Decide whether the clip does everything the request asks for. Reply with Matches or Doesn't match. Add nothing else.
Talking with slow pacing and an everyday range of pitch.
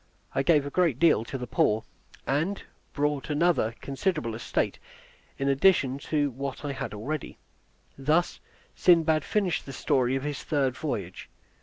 Doesn't match